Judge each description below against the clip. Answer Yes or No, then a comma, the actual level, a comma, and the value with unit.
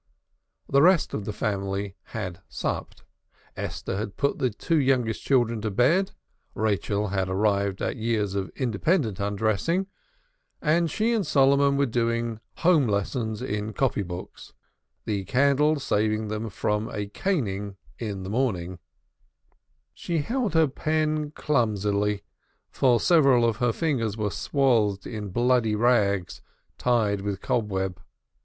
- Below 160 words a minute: Yes, slow, 135 wpm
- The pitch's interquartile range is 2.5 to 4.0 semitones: No, average, 5.3 semitones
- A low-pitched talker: Yes, low, 110 Hz